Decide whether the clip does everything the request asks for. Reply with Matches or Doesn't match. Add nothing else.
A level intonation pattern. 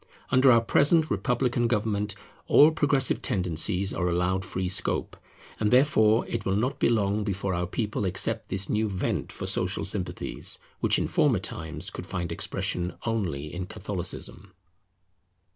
Doesn't match